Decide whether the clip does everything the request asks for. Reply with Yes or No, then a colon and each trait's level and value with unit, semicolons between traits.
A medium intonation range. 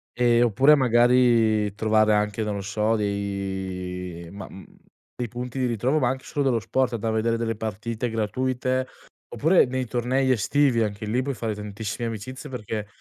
Yes: average, 3.2 semitones